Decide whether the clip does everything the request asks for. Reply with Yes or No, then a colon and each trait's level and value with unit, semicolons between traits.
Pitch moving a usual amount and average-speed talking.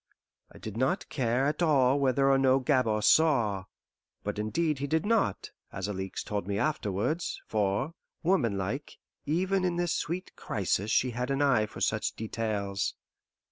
No: wide, 6.6 semitones; average, 155 wpm